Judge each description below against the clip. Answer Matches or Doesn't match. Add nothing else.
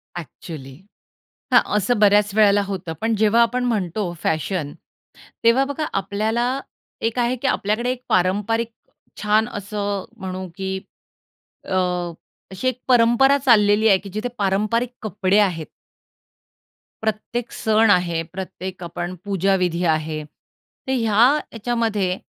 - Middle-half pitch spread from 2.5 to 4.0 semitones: Matches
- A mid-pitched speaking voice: Doesn't match